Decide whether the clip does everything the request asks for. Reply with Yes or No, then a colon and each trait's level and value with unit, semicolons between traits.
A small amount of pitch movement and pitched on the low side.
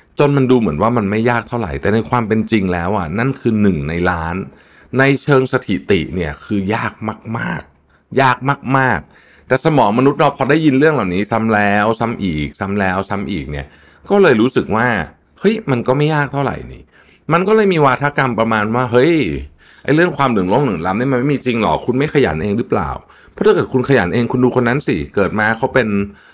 No: average, 4.9 semitones; low, 115 Hz